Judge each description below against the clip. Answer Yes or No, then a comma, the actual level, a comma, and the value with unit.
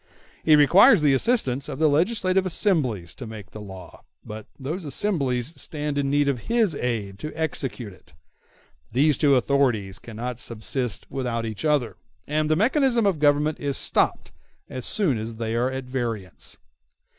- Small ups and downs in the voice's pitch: No, average, 5.1 semitones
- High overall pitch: No, low, 135 Hz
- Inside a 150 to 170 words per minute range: Yes, average, 160 wpm